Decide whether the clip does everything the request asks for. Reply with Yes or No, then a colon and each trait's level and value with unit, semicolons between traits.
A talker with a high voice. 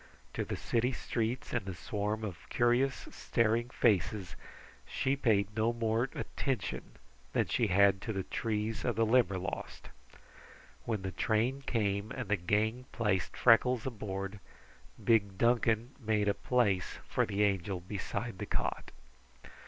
No: low, 110 Hz